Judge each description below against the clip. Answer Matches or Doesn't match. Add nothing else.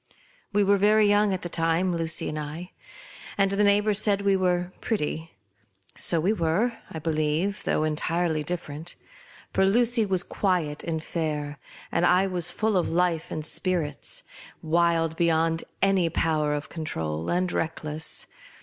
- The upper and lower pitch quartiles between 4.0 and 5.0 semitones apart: Doesn't match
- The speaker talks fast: Doesn't match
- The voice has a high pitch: Doesn't match